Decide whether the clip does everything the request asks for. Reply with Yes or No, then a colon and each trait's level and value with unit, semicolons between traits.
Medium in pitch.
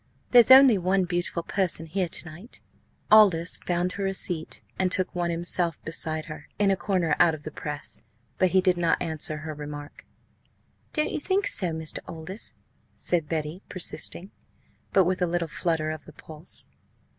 Yes: medium, 175 Hz